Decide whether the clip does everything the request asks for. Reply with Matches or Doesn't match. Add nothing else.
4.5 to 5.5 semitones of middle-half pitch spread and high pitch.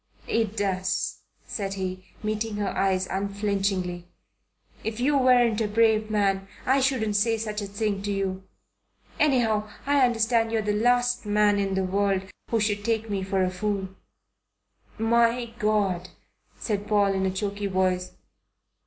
Doesn't match